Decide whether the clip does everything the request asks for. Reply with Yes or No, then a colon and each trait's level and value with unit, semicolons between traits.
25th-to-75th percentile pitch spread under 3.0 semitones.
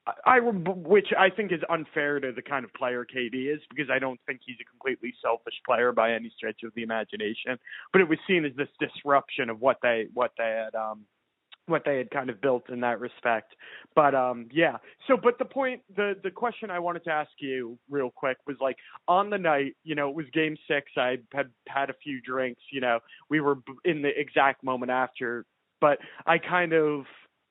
No: average, 4.5 semitones